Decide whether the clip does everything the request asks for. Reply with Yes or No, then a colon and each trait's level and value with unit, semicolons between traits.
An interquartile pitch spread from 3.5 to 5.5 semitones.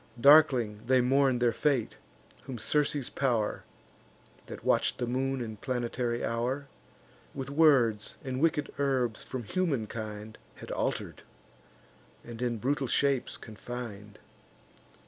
No: average, 3.0 semitones